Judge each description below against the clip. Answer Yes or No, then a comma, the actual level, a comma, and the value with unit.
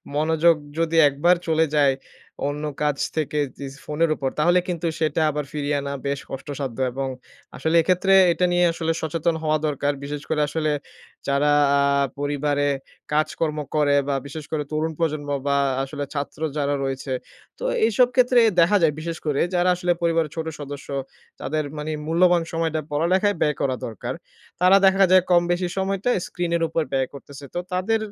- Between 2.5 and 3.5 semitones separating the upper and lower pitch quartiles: Yes, average, 3.0 semitones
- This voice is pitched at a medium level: Yes, medium, 155 Hz